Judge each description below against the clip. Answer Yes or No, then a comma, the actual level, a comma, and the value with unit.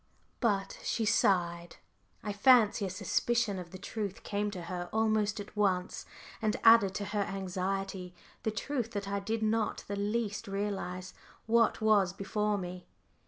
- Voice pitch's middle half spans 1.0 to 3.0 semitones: Yes, narrow, 2.4 semitones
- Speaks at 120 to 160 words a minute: Yes, average, 155 wpm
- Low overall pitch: No, high, 205 Hz